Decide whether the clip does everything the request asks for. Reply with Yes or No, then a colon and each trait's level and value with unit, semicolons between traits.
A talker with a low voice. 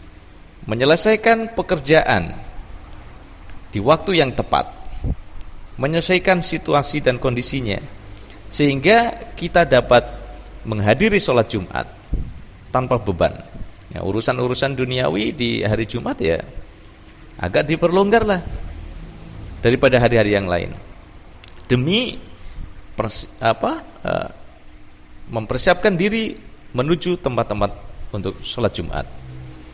Yes: low, 115 Hz